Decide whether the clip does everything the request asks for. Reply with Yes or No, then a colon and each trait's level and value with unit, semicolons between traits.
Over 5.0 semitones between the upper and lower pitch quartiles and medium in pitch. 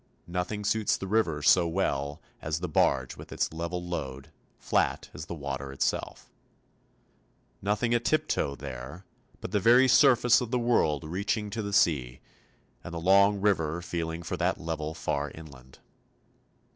No: wide, 5.5 semitones; very low, 85 Hz